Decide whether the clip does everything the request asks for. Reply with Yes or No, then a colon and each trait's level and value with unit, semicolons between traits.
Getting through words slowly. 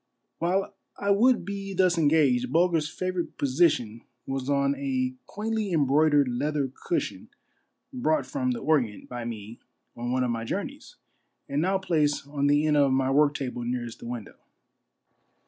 No: average, 155 wpm